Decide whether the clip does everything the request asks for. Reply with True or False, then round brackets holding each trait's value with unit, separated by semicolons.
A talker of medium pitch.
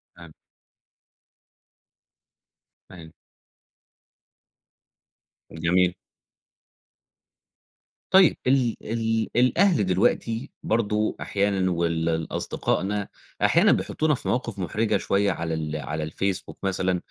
False (100 Hz)